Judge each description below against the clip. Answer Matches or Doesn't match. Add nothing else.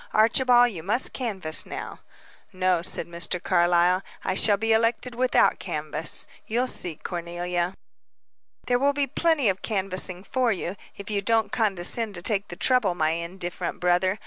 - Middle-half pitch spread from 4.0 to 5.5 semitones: Matches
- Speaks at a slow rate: Doesn't match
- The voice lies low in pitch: Doesn't match